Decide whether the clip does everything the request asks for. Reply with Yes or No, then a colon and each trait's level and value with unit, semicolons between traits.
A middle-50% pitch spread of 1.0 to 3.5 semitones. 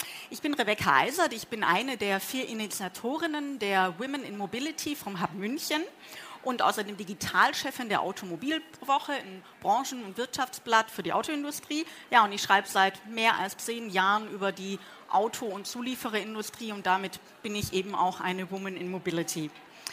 No: average, 5.3 semitones